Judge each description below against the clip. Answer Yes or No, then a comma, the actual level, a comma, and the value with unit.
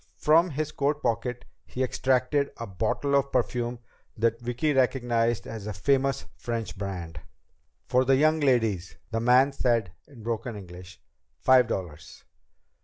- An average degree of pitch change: Yes, average, 3.4 semitones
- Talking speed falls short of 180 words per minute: Yes, average, 140 wpm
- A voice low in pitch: Yes, low, 120 Hz